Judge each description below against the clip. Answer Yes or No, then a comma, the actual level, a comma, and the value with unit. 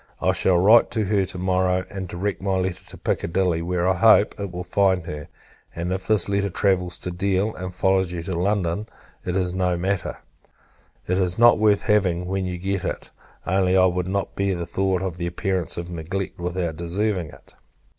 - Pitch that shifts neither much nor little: No, narrow, 1.7 semitones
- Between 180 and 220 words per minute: Yes, average, 200 wpm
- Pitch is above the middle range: No, very low, 95 Hz